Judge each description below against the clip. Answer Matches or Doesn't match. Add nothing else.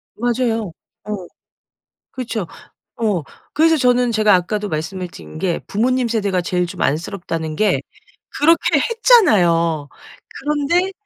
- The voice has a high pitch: Matches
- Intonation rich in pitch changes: Matches